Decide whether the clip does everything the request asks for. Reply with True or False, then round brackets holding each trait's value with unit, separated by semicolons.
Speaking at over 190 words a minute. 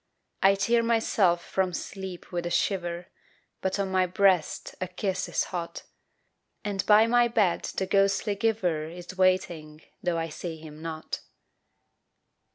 False (145 wpm)